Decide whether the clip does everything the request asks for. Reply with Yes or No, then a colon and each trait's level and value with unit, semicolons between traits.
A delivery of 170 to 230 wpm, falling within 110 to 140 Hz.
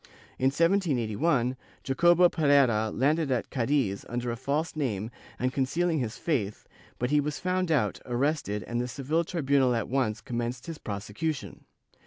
No: average, 150 wpm; low, 135 Hz